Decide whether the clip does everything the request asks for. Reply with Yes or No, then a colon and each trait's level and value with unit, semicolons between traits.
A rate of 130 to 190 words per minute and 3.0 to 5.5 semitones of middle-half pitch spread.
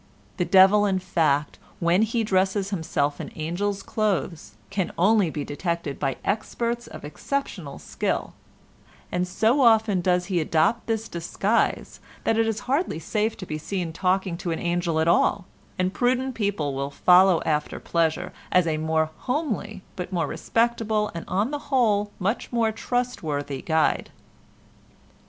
Yes: average, 150 wpm; average, 4.9 semitones